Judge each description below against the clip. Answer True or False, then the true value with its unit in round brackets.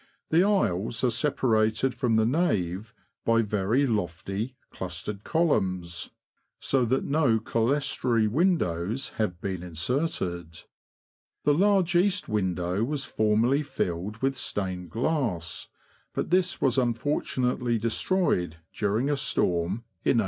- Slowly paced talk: True (120 wpm)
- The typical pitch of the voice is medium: False (115 Hz)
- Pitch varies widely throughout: True (6.6 semitones)